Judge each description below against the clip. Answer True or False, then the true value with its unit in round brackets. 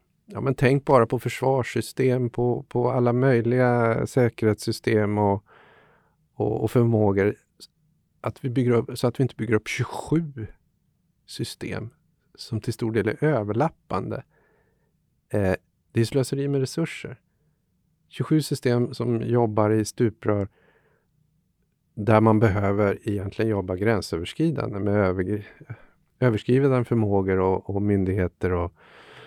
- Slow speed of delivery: True (120 wpm)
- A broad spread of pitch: False (4.1 semitones)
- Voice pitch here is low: True (115 Hz)